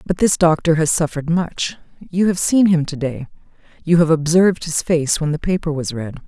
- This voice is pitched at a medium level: Yes, medium, 165 Hz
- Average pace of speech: No, fast, 210 wpm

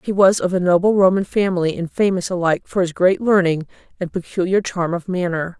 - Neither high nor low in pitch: Yes, medium, 180 Hz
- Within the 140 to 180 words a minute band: No, fast, 205 wpm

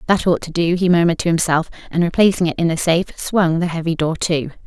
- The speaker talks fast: Yes, fast, 245 wpm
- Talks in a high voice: No, medium, 170 Hz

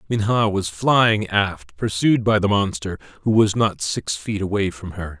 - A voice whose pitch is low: Yes, low, 100 Hz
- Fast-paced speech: No, average, 185 wpm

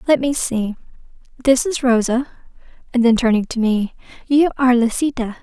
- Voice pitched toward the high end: Yes, high, 245 Hz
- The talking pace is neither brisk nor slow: Yes, average, 155 wpm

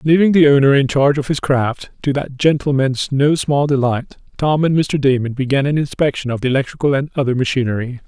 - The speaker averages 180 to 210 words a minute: Yes, average, 200 wpm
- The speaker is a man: Yes, male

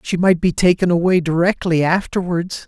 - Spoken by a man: Yes, male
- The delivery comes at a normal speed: Yes, average, 155 wpm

